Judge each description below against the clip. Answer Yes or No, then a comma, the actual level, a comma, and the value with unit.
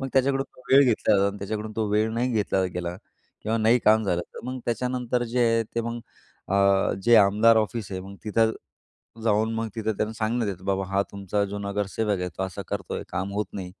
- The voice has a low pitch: Yes, low, 110 Hz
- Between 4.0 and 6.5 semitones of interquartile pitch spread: No, average, 2.7 semitones